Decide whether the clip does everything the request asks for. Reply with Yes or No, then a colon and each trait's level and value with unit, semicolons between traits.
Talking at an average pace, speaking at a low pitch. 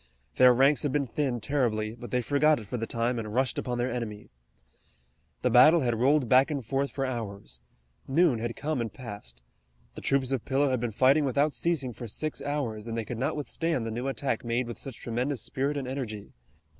No: fast, 210 wpm; low, 125 Hz